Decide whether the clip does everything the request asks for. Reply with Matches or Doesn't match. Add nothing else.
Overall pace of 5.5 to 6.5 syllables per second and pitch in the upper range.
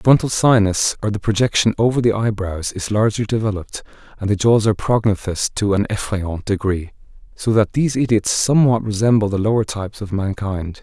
Doesn't match